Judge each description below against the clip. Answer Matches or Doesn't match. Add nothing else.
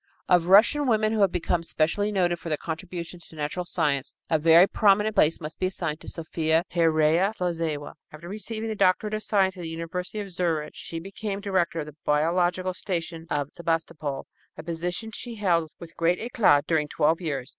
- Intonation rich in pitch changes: Doesn't match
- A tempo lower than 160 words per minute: Doesn't match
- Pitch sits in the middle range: Matches